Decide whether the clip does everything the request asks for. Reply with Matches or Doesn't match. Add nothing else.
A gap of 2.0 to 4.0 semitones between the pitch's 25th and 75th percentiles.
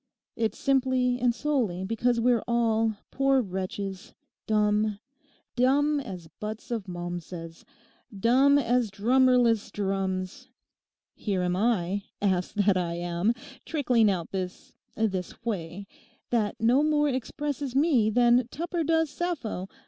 Doesn't match